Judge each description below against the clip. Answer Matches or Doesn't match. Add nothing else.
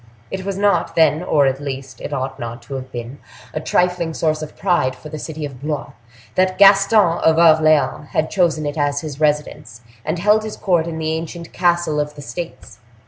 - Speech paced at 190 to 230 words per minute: Matches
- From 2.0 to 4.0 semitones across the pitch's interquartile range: Matches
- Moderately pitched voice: Matches